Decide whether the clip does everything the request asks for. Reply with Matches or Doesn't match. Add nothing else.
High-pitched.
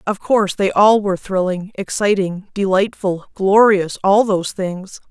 Matches